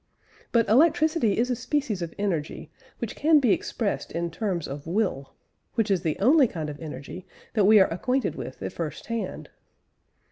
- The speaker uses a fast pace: No, average, 175 wpm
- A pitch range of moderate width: No, wide, 6.7 semitones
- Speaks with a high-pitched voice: Yes, high, 210 Hz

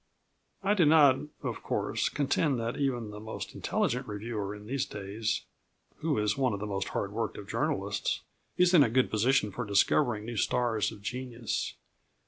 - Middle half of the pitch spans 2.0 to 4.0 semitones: No, average, 4.4 semitones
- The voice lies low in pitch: Yes, low, 120 Hz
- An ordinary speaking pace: Yes, average, 175 wpm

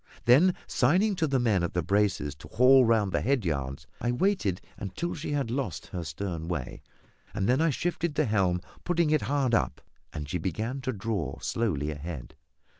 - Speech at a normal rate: Yes, average, 185 wpm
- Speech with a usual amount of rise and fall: No, wide, 8.1 semitones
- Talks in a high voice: No, low, 110 Hz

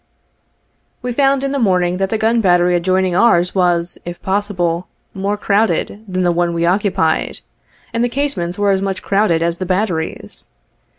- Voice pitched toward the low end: No, high, 190 Hz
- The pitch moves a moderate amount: Yes, average, 3.2 semitones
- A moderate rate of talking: Yes, average, 175 wpm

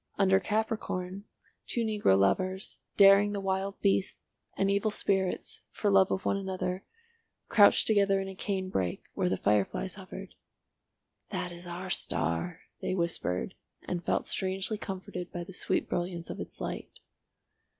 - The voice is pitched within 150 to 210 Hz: Yes, high, 190 Hz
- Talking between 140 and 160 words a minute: Yes, average, 150 wpm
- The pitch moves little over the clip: Yes, narrow, 2.1 semitones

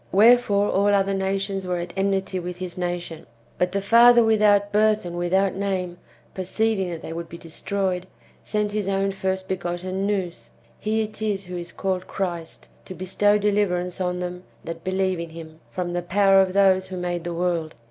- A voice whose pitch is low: No, high, 190 Hz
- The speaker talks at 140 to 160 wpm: No, average, 185 wpm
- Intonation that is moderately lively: No, narrow, 2.1 semitones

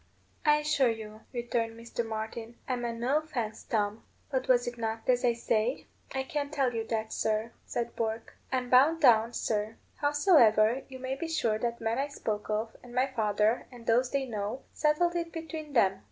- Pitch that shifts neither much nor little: Yes, average, 3.4 semitones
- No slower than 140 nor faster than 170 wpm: No, average, 190 wpm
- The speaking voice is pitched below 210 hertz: No, high, 240 Hz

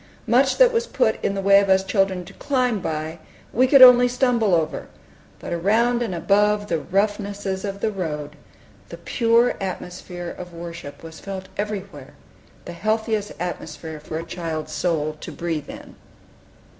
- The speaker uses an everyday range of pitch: Yes, average, 4.6 semitones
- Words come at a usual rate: Yes, average, 160 wpm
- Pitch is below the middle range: No, high, 195 Hz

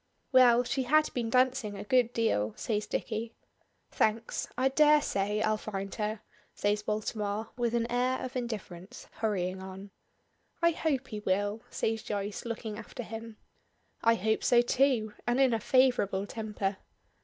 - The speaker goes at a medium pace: Yes, average, 155 wpm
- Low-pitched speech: No, high, 225 Hz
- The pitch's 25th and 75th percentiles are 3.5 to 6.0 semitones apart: No, average, 3.0 semitones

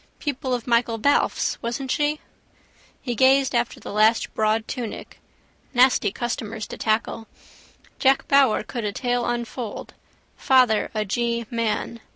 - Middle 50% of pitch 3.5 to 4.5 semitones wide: No, average, 2.7 semitones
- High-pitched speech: Yes, high, 235 Hz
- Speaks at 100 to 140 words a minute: Yes, slow, 135 wpm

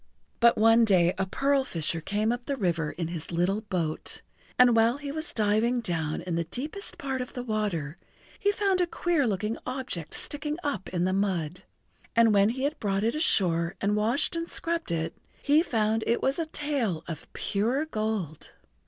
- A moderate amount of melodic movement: No, wide, 7.1 semitones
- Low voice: No, high, 220 Hz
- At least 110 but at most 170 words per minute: No, average, 190 wpm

